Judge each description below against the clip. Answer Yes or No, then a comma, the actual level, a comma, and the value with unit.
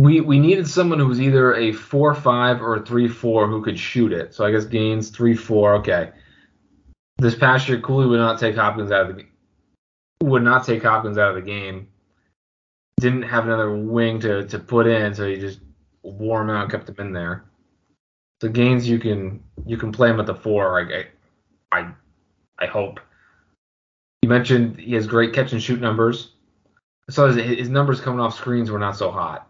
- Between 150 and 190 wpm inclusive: No, average, 200 wpm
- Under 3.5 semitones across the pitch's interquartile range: Yes, average, 2.9 semitones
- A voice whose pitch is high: No, low, 115 Hz